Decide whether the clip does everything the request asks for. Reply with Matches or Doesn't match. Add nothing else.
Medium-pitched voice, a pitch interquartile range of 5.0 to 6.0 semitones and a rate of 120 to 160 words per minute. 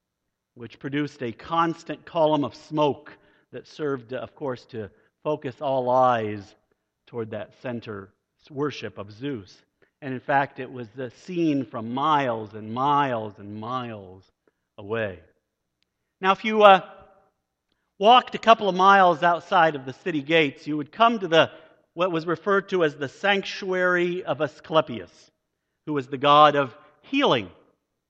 Matches